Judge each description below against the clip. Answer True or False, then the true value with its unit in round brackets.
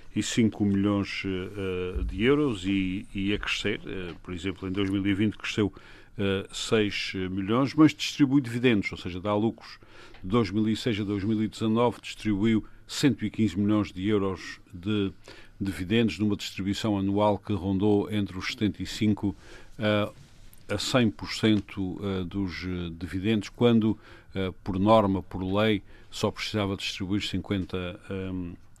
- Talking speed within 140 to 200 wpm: False (125 wpm)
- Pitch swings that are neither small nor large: False (2.2 semitones)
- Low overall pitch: True (105 Hz)